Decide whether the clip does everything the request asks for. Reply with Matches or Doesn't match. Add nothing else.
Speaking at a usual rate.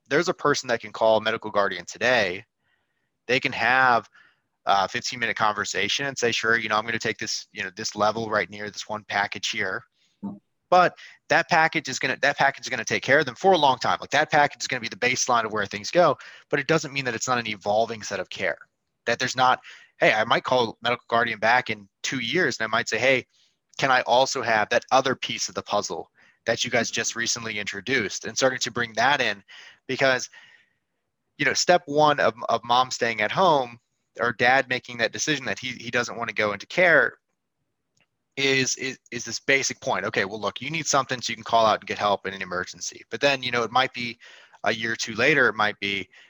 Doesn't match